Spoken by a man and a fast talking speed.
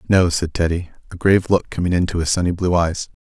Yes: male; fast, 225 wpm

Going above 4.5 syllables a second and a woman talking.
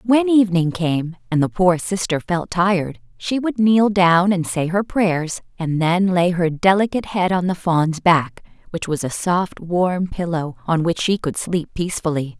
No: 4.4 syllables/s; female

